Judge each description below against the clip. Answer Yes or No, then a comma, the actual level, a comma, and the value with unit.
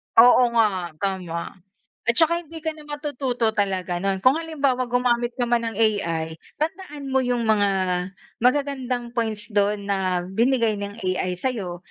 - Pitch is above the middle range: Yes, high, 235 Hz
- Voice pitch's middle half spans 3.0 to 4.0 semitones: No, average, 4.8 semitones